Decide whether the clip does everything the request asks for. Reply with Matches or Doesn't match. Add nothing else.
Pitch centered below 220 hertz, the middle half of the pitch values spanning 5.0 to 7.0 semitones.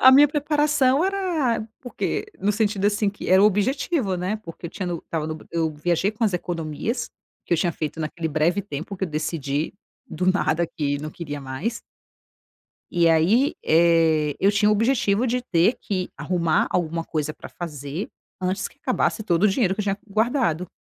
Matches